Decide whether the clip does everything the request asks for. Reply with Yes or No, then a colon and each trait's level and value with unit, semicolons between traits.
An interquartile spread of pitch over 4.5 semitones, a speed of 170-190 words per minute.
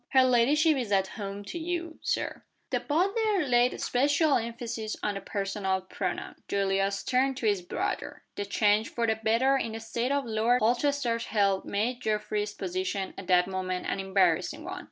Yes: average, 5.2 semitones; average, 175 wpm